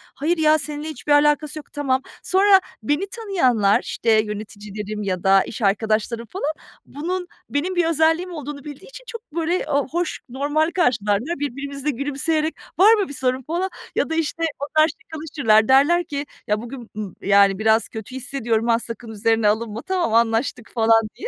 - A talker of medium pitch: No, very high, 280 Hz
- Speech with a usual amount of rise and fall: No, wide, 6.3 semitones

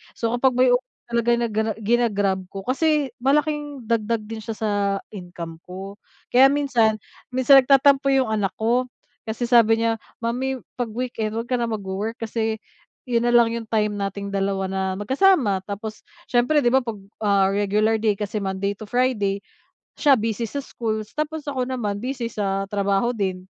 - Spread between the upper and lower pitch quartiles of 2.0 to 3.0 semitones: No, average, 3.8 semitones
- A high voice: Yes, high, 225 Hz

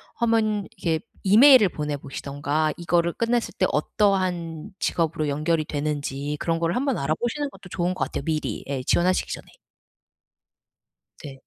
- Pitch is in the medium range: Yes, medium, 165 Hz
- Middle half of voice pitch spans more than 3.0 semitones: Yes, average, 5.1 semitones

